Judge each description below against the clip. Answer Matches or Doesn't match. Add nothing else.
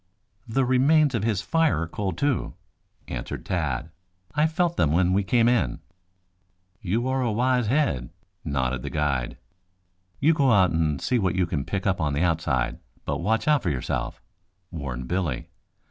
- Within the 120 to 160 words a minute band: Doesn't match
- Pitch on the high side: Doesn't match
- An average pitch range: Doesn't match